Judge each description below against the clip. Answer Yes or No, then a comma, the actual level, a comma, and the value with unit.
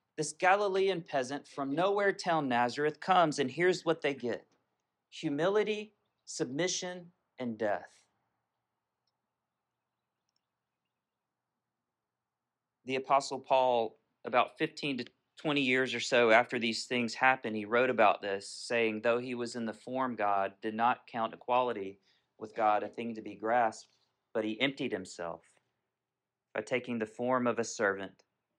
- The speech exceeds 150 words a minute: No, slow, 135 wpm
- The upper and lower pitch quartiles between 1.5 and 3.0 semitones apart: No, average, 5.2 semitones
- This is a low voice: Yes, low, 125 Hz